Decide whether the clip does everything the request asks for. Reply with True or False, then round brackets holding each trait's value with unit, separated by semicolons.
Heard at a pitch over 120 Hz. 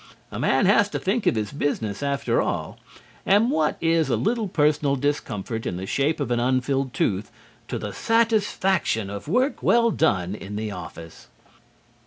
True (140 Hz)